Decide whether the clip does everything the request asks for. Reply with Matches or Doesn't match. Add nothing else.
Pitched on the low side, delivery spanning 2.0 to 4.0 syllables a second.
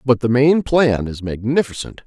Doesn't match